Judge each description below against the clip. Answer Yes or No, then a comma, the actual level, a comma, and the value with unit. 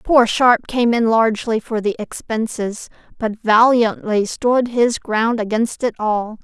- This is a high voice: Yes, high, 225 Hz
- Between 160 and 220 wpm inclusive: No, average, 150 wpm